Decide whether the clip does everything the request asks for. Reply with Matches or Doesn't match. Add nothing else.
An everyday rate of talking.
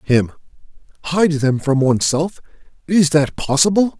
Doesn't match